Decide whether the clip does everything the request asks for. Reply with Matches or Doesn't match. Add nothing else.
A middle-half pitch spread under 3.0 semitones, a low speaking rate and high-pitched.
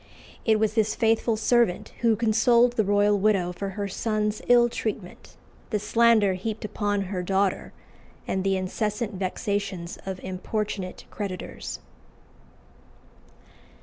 Matches